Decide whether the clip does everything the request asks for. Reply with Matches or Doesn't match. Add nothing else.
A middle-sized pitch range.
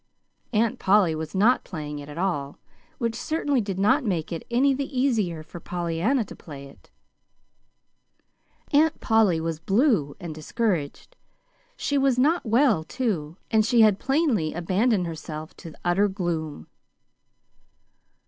Doesn't match